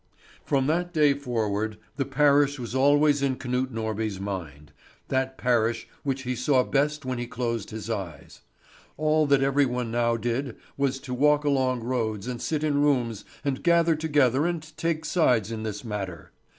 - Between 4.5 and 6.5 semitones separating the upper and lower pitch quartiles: No, average, 4.1 semitones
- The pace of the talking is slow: No, average, 170 wpm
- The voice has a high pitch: No, low, 130 Hz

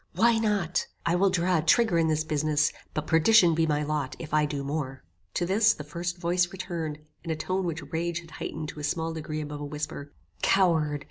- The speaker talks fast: Yes, fast, 215 wpm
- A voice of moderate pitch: Yes, medium, 160 Hz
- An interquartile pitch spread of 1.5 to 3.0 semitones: Yes, average, 2.7 semitones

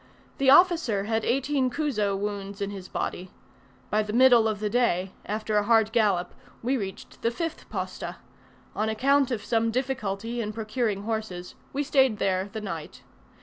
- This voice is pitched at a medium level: No, high, 220 Hz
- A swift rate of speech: No, average, 165 wpm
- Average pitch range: Yes, average, 3.7 semitones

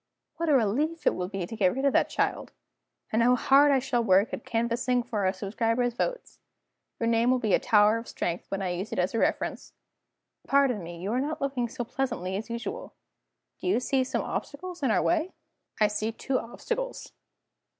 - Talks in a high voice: Yes, high, 235 Hz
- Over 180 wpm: Yes, average, 200 wpm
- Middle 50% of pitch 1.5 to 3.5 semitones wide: No, average, 4.6 semitones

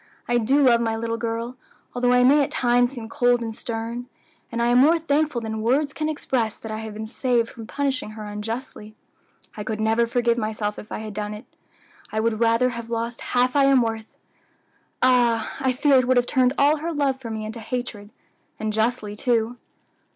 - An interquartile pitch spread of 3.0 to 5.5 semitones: No, narrow, 2.4 semitones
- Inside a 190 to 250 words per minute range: Yes, fast, 205 wpm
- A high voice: Yes, high, 235 Hz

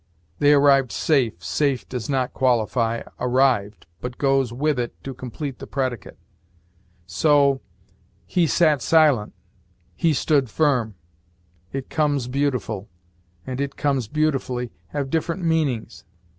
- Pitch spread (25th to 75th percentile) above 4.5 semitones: No, average, 3.1 semitones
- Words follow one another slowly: Yes, slow, 120 wpm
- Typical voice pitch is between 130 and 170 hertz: Yes, low, 135 Hz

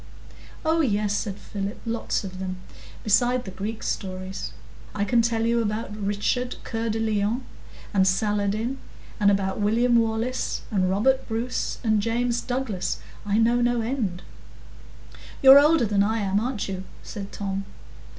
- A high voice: Yes, high, 220 Hz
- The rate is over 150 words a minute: No, average, 145 wpm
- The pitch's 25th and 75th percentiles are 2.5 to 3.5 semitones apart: Yes, average, 3.0 semitones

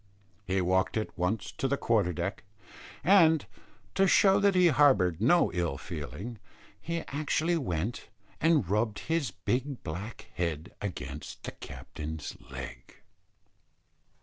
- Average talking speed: No, slow, 125 wpm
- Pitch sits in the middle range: No, low, 110 Hz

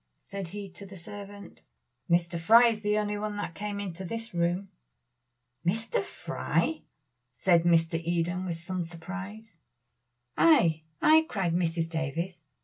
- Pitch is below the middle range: No, medium, 185 Hz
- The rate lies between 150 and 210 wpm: No, average, 140 wpm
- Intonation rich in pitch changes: No, average, 3.4 semitones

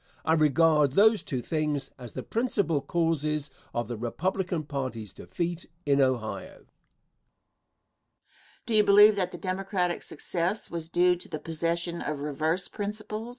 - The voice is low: No, medium, 165 Hz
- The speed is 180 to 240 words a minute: No, average, 145 wpm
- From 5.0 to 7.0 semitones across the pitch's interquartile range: No, average, 4.4 semitones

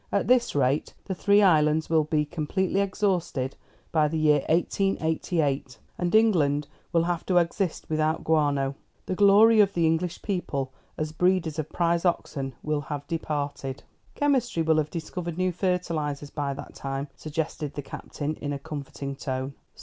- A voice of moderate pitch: Yes, medium, 160 Hz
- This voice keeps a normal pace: Yes, average, 155 wpm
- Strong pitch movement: No, average, 3.8 semitones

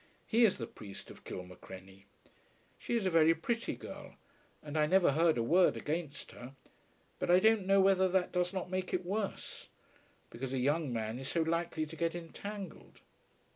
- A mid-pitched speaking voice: Yes, medium, 165 Hz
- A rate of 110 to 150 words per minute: No, average, 180 wpm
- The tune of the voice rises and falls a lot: Yes, wide, 5.7 semitones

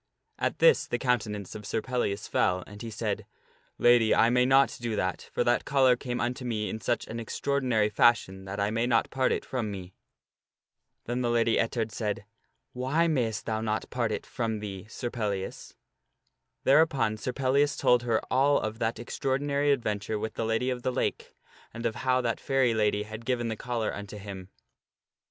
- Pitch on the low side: Yes, low, 115 Hz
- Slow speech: No, average, 190 wpm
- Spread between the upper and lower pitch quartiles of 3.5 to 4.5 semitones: No, average, 3.0 semitones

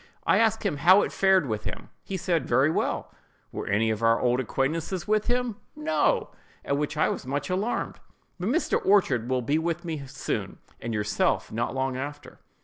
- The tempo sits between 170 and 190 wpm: Yes, average, 180 wpm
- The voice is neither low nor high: Yes, medium, 150 Hz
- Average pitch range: No, wide, 6.9 semitones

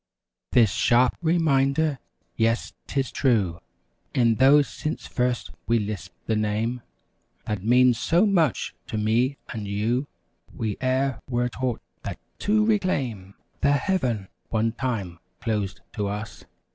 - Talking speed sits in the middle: No, slow, 130 wpm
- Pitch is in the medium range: No, low, 120 Hz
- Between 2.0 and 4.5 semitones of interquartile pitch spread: Yes, average, 4.2 semitones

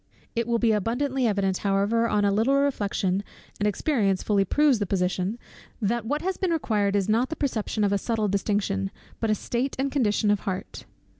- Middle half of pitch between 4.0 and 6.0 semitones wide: No, average, 3.6 semitones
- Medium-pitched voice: No, high, 215 Hz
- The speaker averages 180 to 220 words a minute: Yes, average, 195 wpm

